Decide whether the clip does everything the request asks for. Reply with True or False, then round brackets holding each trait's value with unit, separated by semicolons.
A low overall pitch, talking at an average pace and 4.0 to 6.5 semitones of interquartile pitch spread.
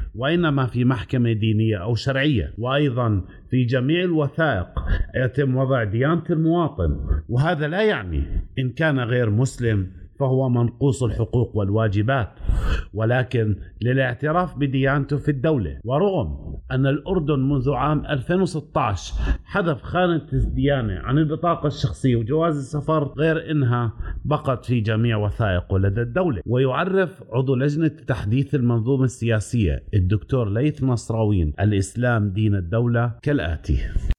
True (125 Hz; 115 wpm; 5.4 semitones)